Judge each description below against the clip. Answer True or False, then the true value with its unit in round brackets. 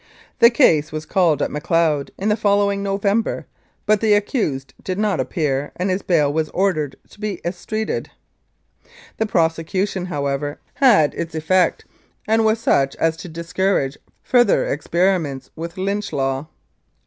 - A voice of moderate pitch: True (180 Hz)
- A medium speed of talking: True (145 wpm)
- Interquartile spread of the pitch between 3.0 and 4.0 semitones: False (5.0 semitones)